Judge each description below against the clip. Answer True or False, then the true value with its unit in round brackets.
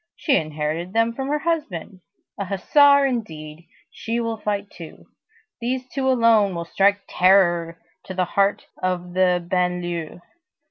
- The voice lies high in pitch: True (195 Hz)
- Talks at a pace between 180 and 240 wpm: False (140 wpm)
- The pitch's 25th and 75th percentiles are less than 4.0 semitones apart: False (5.0 semitones)